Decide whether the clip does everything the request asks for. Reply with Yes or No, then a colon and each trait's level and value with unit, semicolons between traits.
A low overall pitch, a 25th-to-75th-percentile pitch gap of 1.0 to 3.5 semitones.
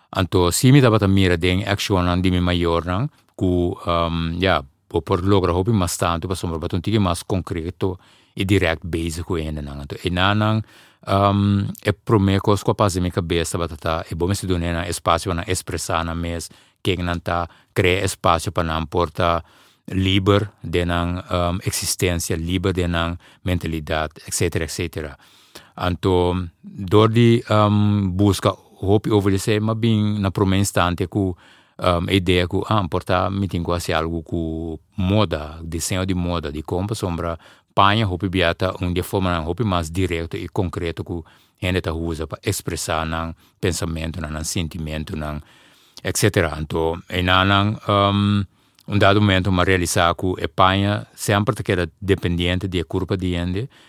Yes: very low, 90 Hz; average, 2.9 semitones